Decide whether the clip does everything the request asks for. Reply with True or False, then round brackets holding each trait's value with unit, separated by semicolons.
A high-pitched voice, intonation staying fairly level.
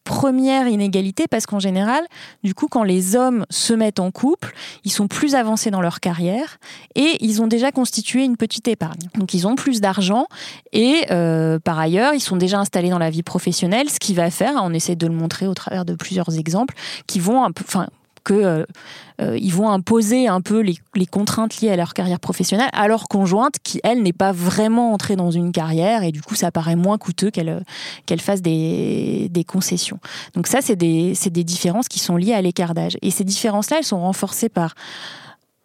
False (195 Hz; 4.1 semitones)